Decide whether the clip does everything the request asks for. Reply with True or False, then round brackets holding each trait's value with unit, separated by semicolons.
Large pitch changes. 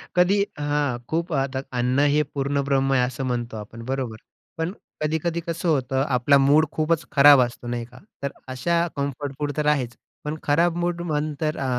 False (3.2 semitones)